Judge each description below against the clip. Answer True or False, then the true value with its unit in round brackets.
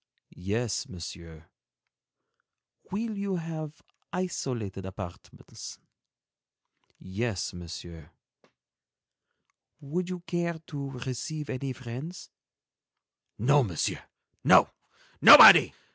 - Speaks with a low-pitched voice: True (130 Hz)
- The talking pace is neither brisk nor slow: False (75 wpm)